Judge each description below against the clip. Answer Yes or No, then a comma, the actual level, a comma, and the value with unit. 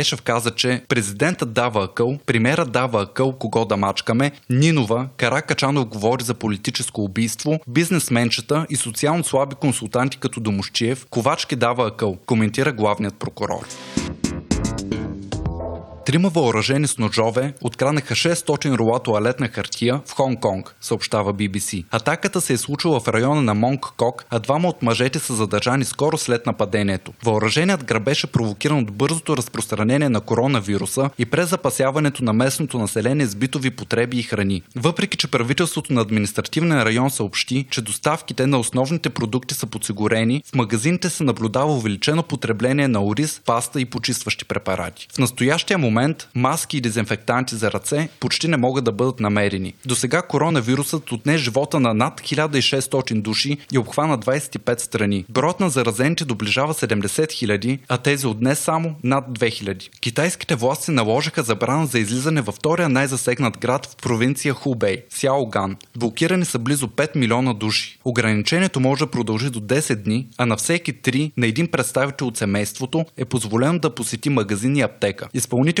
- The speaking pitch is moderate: No, low, 125 Hz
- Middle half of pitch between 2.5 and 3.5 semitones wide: No, average, 4.1 semitones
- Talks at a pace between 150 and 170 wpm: Yes, average, 155 wpm